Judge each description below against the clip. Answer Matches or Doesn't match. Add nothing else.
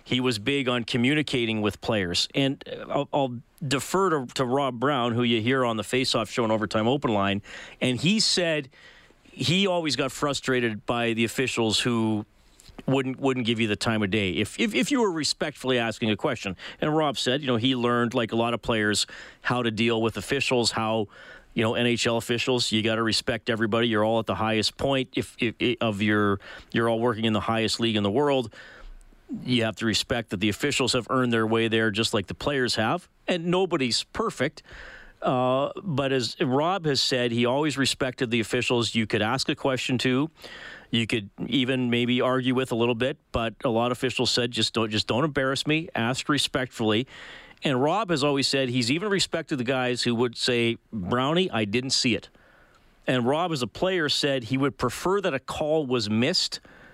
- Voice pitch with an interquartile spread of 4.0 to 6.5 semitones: Doesn't match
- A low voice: Matches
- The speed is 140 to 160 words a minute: Doesn't match